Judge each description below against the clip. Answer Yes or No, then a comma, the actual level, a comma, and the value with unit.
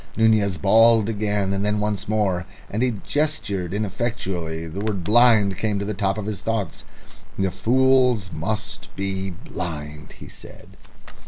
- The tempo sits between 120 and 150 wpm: No, average, 160 wpm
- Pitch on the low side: Yes, low, 100 Hz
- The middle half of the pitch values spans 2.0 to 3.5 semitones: Yes, narrow, 2.6 semitones